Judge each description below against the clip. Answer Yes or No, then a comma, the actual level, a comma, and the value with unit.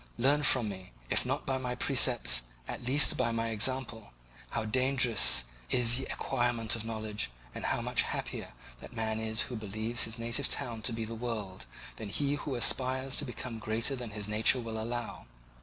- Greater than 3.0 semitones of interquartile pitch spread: No, narrow, 2.6 semitones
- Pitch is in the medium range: No, low, 115 Hz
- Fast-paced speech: No, average, 185 wpm